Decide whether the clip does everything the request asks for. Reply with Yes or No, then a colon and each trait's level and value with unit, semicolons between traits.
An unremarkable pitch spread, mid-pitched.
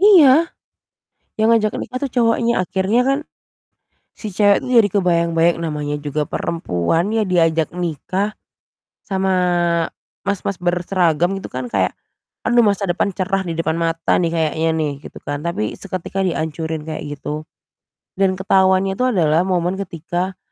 Yes: average, 3.5 semitones; medium, 180 Hz